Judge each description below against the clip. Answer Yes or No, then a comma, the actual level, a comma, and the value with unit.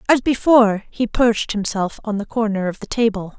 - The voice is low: No, high, 220 Hz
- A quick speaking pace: No, average, 195 wpm